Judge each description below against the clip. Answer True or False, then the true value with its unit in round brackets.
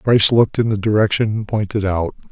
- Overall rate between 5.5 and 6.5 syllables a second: True (5.6 syllables/s)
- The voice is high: False (105 Hz)